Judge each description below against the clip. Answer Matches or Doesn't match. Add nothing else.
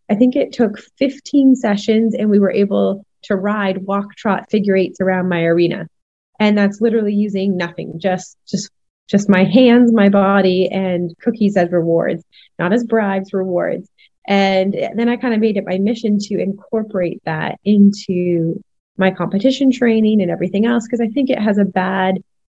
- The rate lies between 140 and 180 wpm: Matches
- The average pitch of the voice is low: Doesn't match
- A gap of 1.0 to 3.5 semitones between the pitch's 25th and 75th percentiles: Matches